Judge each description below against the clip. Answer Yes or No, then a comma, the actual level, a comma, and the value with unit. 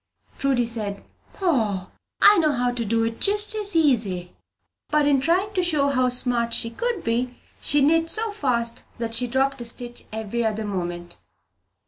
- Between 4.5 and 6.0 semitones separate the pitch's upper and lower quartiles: Yes, average, 5.1 semitones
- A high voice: Yes, high, 245 Hz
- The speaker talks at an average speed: Yes, average, 175 wpm